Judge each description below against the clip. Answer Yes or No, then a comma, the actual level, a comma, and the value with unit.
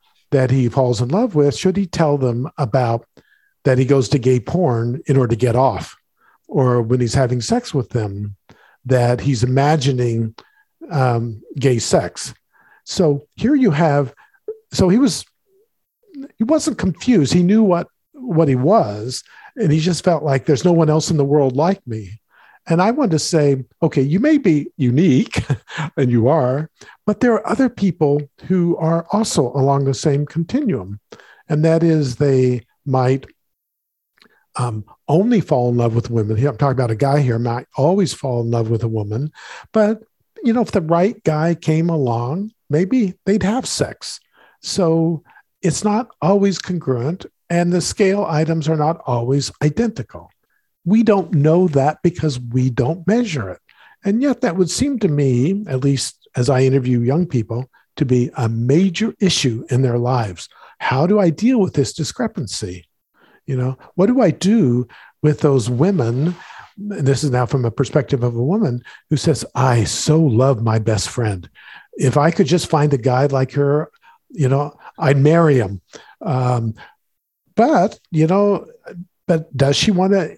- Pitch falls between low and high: Yes, medium, 150 Hz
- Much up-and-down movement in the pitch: Yes, wide, 6.1 semitones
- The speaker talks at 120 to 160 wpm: No, average, 170 wpm